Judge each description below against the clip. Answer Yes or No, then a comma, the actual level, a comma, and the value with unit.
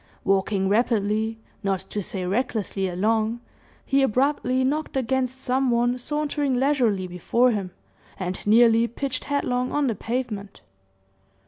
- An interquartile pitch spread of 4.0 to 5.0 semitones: Yes, average, 4.3 semitones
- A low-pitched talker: No, high, 235 Hz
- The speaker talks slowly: Yes, slow, 125 wpm